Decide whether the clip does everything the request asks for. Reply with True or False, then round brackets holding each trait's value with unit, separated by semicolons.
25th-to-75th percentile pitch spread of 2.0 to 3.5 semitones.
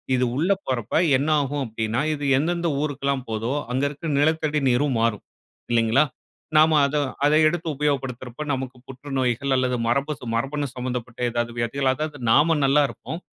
True (3.2 semitones)